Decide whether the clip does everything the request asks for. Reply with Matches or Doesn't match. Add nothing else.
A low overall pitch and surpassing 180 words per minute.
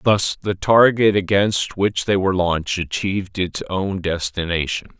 Doesn't match